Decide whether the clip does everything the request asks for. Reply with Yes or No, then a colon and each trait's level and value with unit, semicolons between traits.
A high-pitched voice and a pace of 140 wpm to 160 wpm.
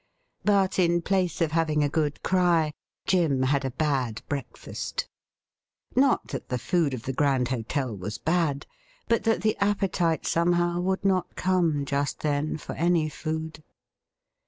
No: medium, 160 Hz; average, 150 wpm